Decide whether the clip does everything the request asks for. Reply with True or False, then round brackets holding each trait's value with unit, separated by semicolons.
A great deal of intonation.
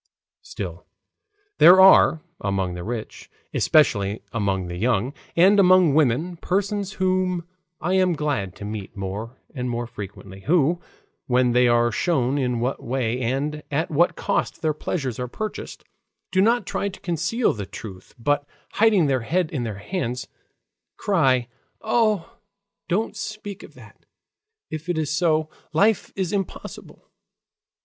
True (7.5 semitones)